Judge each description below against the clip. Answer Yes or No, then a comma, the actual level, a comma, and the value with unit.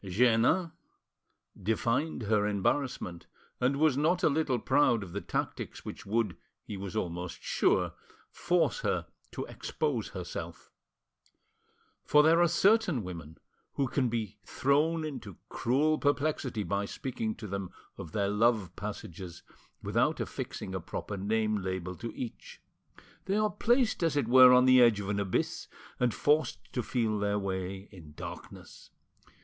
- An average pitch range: No, wide, 6.5 semitones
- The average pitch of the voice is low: Yes, low, 115 Hz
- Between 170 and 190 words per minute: No, average, 145 wpm